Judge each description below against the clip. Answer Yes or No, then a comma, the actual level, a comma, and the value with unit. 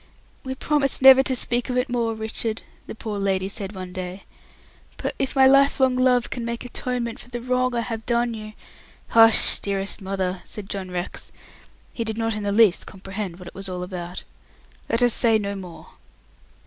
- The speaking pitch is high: Yes, high, 225 Hz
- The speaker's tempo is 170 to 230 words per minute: Yes, average, 195 wpm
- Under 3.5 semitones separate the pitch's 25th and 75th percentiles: No, average, 4.1 semitones